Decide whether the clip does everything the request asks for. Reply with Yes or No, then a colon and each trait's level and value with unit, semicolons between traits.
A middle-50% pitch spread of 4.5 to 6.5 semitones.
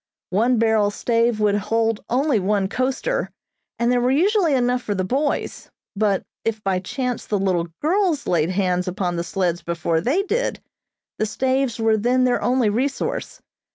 Yes: average, 4.9 semitones